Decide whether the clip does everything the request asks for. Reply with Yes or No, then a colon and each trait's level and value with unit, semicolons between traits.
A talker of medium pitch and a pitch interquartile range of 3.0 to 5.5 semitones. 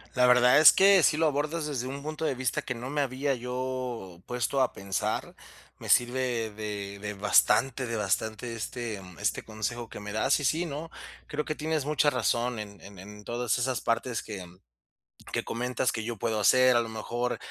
No: low, 125 Hz; average, 3.7 semitones